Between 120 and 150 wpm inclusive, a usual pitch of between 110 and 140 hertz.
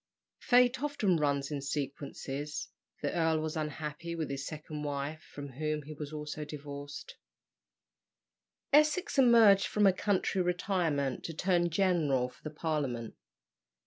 No: slow, 135 wpm; medium, 155 Hz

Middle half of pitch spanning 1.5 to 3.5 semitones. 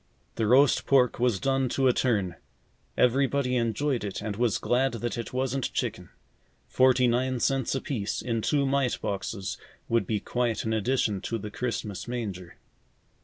Yes: average, 3.1 semitones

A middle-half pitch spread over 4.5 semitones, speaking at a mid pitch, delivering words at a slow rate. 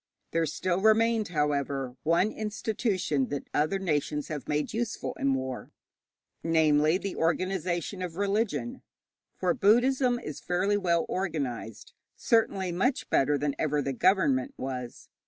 Yes: wide, 5.5 semitones; medium, 170 Hz; slow, 130 wpm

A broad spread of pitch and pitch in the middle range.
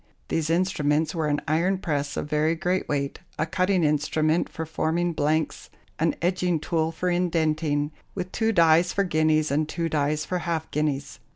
No: narrow, 2.4 semitones; medium, 160 Hz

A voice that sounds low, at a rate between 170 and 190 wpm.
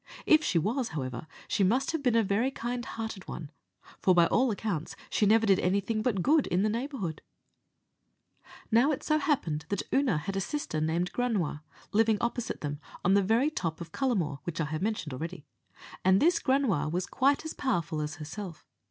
No: high, 200 Hz; average, 185 wpm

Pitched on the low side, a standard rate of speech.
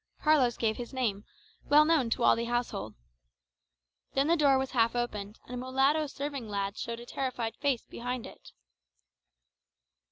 No: high, 245 Hz; average, 160 wpm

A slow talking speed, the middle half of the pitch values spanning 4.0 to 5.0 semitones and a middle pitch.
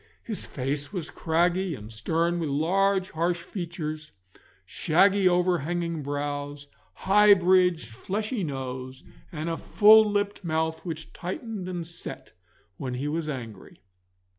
Yes: slow, 130 wpm; average, 4.3 semitones; medium, 170 Hz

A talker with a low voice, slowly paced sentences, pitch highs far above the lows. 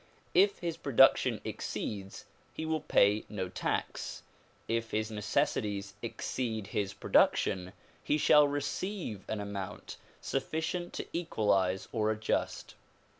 Yes: low, 110 Hz; slow, 115 wpm; wide, 6.8 semitones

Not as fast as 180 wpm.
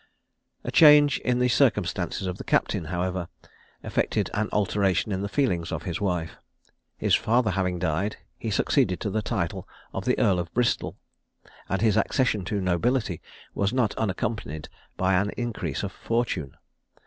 Yes: average, 160 wpm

